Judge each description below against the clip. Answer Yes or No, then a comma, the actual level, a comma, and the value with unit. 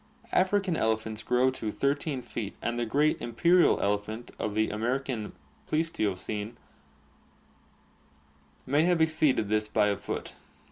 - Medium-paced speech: No, slow, 125 wpm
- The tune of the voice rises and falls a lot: Yes, wide, 6.1 semitones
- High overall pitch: No, low, 120 Hz